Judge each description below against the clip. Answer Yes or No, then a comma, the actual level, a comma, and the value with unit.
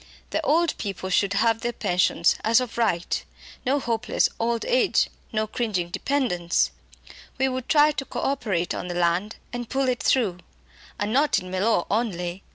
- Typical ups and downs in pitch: No, wide, 5.9 semitones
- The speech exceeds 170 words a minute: No, average, 165 wpm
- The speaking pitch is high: Yes, high, 225 Hz